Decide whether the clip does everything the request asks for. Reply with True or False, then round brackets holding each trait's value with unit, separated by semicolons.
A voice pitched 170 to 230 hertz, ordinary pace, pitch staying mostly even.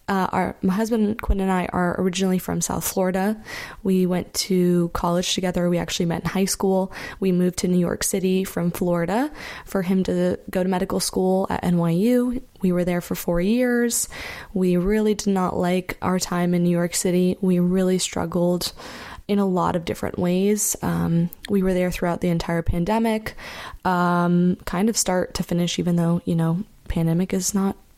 True (185 Hz; 185 wpm; 1.7 semitones)